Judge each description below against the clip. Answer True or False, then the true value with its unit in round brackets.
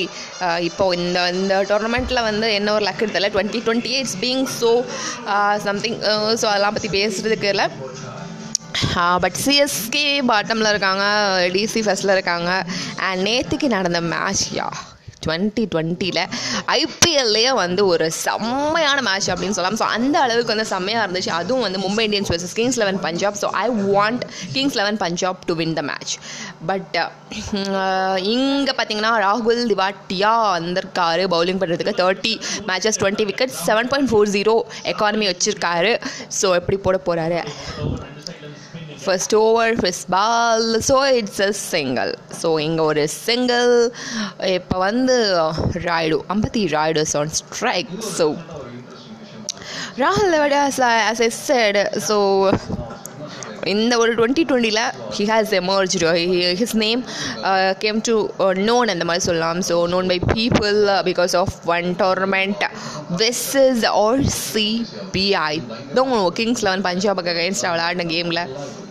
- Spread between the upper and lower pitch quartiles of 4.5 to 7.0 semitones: False (4.1 semitones)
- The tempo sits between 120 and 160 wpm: True (125 wpm)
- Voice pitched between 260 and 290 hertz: False (200 Hz)